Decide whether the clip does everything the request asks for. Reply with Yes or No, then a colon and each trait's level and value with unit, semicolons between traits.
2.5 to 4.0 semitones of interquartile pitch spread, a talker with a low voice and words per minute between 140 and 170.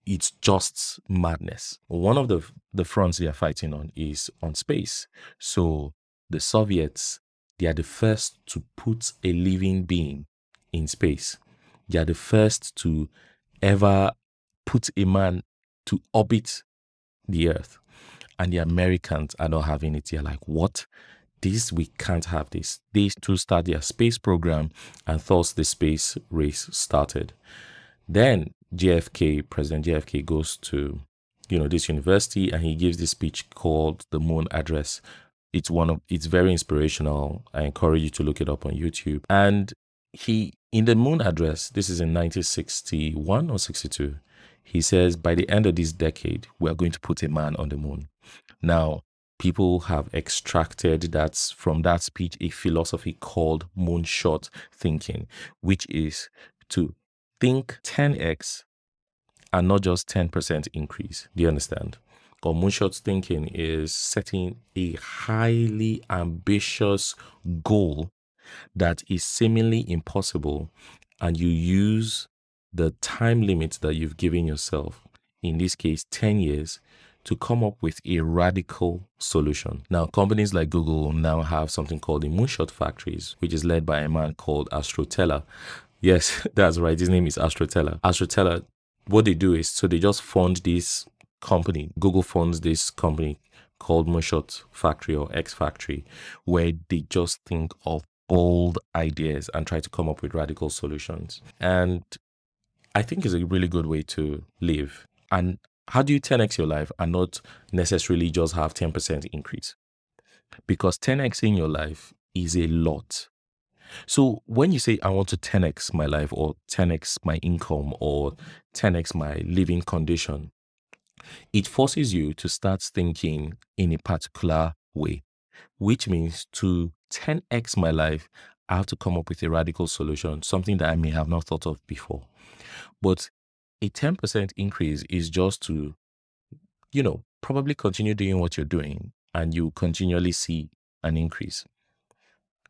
Yes: average, 3.6 semitones; very low, 85 Hz; average, 150 wpm